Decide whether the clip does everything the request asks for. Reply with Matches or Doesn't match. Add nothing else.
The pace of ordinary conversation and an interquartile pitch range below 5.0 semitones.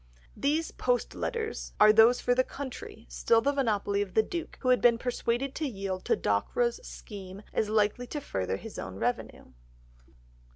Doesn't match